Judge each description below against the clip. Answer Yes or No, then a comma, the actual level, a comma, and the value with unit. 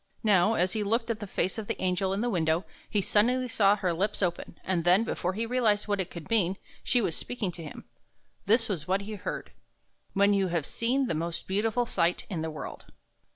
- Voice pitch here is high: Yes, high, 200 Hz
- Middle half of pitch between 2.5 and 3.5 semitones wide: No, average, 3.9 semitones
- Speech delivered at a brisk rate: Yes, fast, 225 wpm